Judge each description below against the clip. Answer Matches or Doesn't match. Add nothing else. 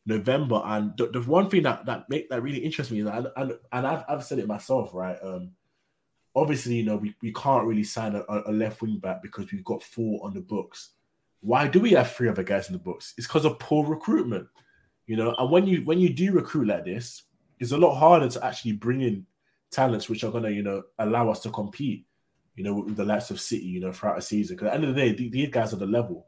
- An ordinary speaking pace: Doesn't match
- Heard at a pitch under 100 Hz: Doesn't match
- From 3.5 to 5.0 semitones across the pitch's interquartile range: Matches